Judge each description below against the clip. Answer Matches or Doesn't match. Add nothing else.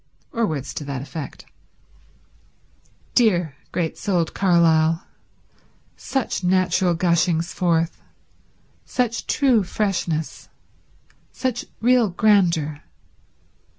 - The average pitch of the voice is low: Doesn't match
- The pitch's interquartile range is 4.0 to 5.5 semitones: Matches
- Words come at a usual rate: Doesn't match